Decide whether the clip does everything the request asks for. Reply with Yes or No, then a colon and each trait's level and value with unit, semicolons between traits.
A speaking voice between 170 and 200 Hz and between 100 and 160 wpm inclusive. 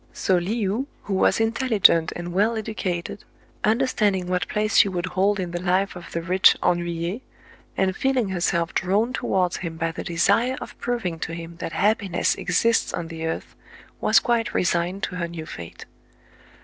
No: medium, 185 Hz; average, 175 wpm